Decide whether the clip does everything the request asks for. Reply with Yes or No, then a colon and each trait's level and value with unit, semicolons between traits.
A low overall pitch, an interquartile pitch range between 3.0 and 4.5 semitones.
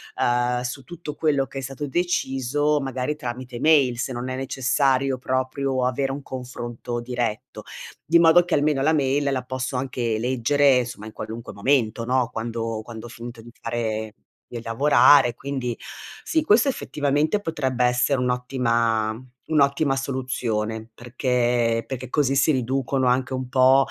No: low, 130 Hz; narrow, 2.5 semitones